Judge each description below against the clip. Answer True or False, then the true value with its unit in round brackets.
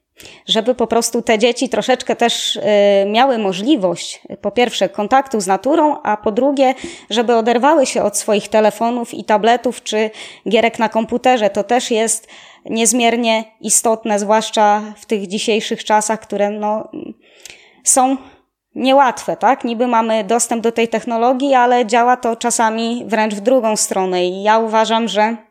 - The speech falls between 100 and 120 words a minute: False (145 wpm)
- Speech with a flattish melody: True (2.3 semitones)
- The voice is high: True (230 Hz)